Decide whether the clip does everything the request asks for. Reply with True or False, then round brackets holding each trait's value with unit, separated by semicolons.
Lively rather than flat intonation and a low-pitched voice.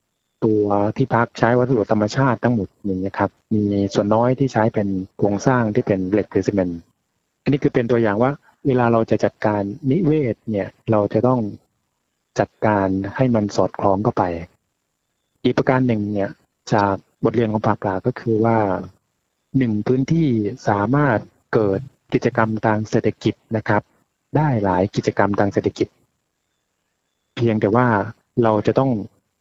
False (3.6 semitones; 110 Hz)